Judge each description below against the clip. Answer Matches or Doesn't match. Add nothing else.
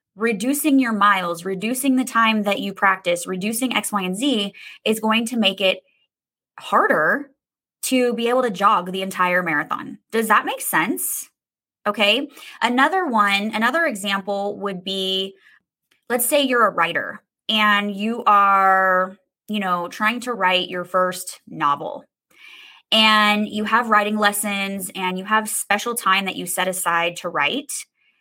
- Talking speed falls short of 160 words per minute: Matches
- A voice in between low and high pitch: Doesn't match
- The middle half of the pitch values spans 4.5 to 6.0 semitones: Doesn't match